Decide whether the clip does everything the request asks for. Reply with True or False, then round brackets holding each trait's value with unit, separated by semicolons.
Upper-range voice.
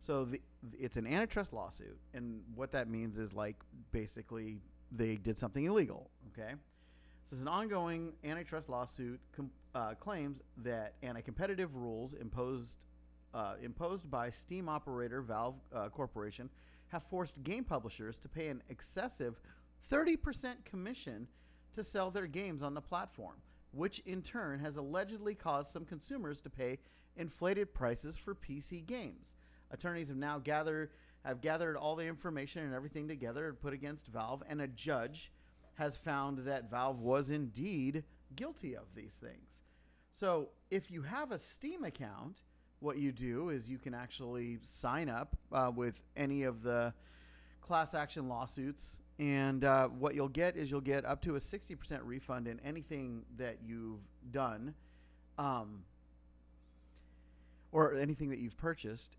False (135 Hz)